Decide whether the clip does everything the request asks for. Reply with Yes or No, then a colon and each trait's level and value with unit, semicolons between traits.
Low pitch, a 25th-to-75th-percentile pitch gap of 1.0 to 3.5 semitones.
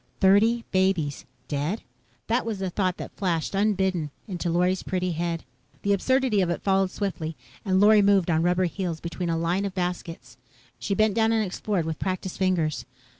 No: medium, 185 Hz; average, 2.8 semitones